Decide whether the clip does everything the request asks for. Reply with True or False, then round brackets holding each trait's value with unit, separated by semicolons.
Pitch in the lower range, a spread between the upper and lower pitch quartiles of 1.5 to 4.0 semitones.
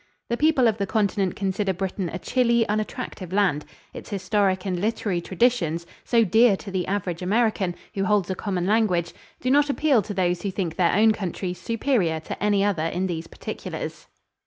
False (195 Hz; 3.5 semitones)